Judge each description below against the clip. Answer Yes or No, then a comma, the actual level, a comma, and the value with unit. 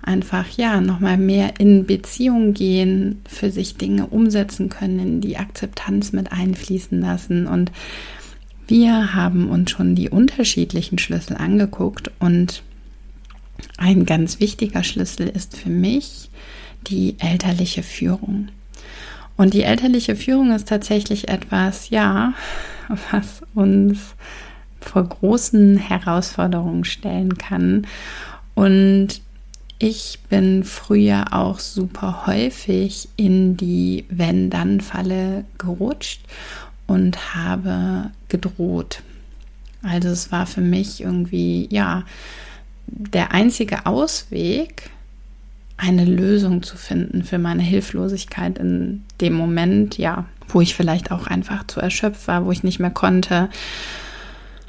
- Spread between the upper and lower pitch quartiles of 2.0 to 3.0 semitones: Yes, narrow, 2.6 semitones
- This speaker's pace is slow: Yes, slow, 110 wpm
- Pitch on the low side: No, high, 190 Hz